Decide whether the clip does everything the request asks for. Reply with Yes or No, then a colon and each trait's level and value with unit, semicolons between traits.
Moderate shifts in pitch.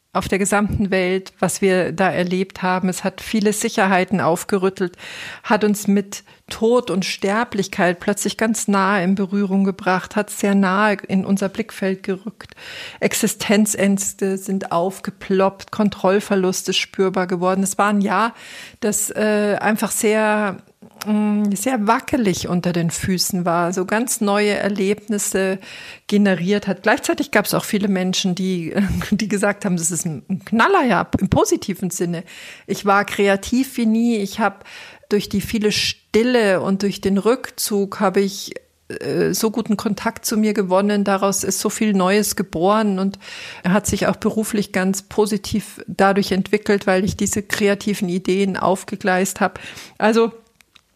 No: narrow, 1.8 semitones